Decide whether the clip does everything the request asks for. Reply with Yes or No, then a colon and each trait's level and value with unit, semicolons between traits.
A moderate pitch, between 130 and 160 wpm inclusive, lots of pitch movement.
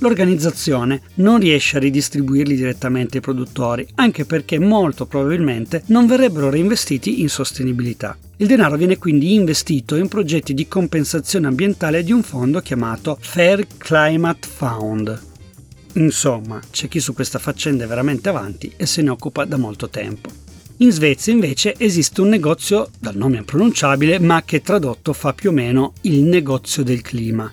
No: medium, 145 Hz; average, 155 wpm; average, 5.0 semitones